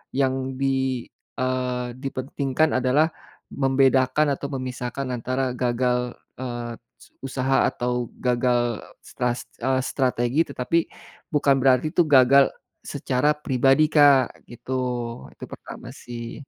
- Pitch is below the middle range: Yes, low, 130 Hz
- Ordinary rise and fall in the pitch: No, narrow, 1.7 semitones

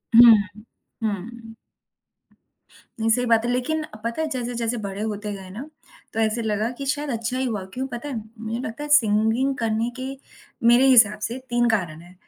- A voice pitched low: No, high, 230 Hz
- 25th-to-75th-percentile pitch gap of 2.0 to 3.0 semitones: Yes, narrow, 2.5 semitones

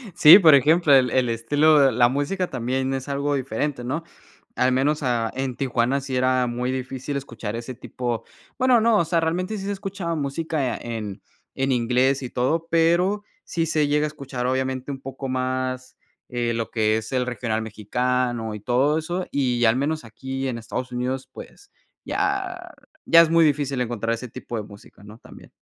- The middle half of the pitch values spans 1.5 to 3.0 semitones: No, average, 3.9 semitones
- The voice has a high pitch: No, low, 130 Hz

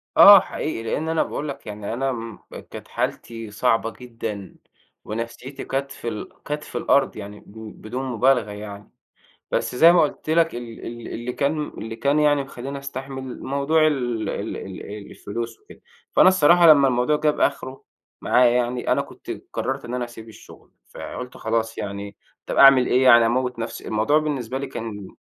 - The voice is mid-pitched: No, low, 125 Hz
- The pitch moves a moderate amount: Yes, average, 3.5 semitones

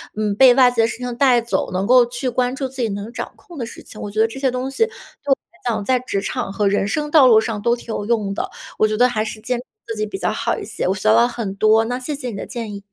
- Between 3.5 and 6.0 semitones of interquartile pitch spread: No, average, 2.9 semitones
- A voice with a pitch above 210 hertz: Yes, high, 235 Hz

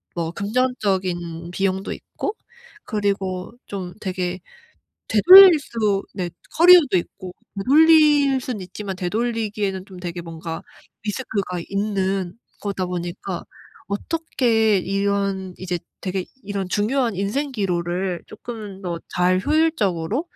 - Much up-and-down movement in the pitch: No, average, 3.8 semitones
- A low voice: No, high, 195 Hz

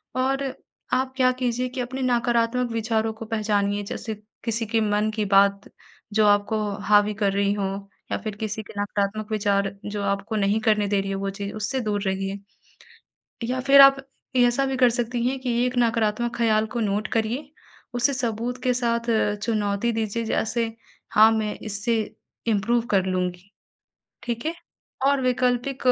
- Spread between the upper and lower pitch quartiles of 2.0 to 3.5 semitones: Yes, average, 3.0 semitones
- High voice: Yes, high, 220 Hz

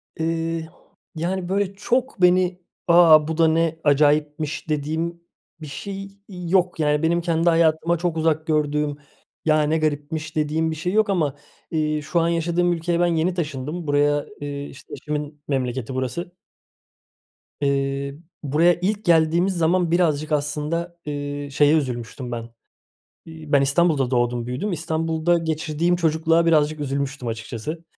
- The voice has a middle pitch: Yes, medium, 160 Hz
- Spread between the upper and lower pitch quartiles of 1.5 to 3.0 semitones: Yes, average, 2.7 semitones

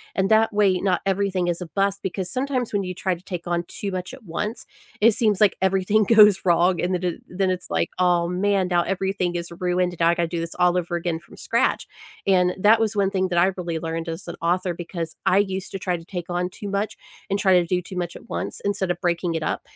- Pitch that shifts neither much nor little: No, narrow, 2.2 semitones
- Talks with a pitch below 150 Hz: No, medium, 180 Hz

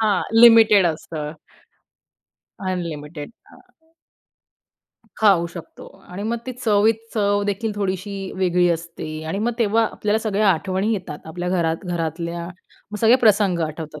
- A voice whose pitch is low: No, high, 190 Hz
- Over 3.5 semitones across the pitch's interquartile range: Yes, average, 4.0 semitones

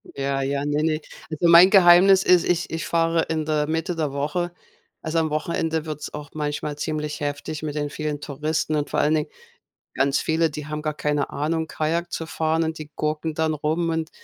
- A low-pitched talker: No, medium, 155 Hz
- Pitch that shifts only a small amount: Yes, narrow, 1.6 semitones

